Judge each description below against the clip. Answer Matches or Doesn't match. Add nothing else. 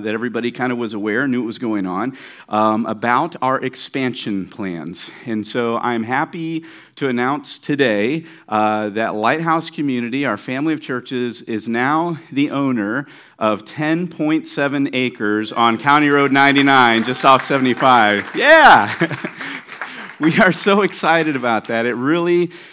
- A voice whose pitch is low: Matches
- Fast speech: Doesn't match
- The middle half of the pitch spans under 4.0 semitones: Doesn't match